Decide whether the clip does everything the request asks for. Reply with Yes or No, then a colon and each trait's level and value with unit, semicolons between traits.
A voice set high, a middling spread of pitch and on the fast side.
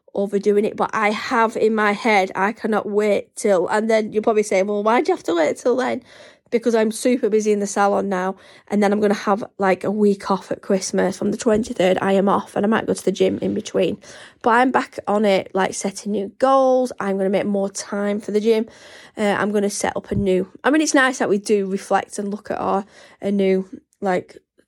No: high, 205 Hz; narrow, 2.2 semitones; fast, 250 wpm